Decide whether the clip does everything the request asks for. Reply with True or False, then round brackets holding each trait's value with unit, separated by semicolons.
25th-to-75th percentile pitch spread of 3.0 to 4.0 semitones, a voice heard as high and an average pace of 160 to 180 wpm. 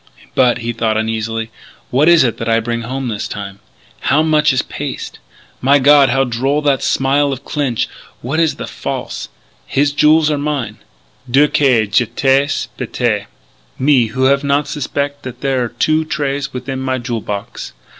False (3.5 semitones; 135 Hz; 170 wpm)